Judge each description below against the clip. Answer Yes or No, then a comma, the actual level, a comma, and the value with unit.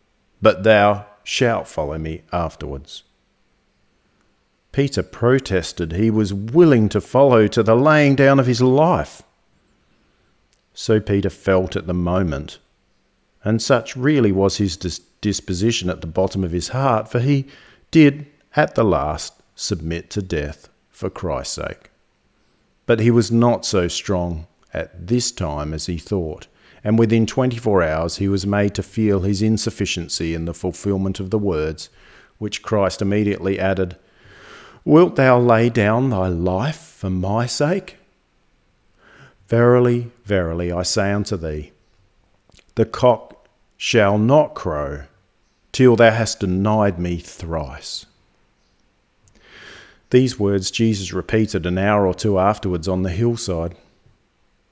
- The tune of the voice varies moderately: Yes, average, 4.2 semitones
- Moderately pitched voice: No, low, 100 Hz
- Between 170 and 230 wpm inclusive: No, slow, 135 wpm